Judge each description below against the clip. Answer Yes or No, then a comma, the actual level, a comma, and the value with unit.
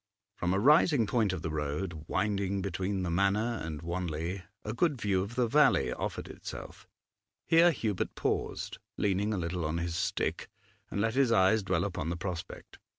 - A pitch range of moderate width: Yes, average, 4.2 semitones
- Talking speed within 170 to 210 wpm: Yes, average, 175 wpm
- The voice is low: Yes, very low, 95 Hz